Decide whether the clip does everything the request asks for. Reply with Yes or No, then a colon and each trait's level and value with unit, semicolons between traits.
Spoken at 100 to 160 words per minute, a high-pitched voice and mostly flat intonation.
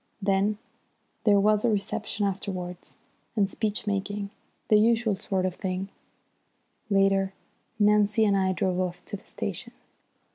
Yes: slow, 135 wpm; high, 200 Hz; narrow, 1.6 semitones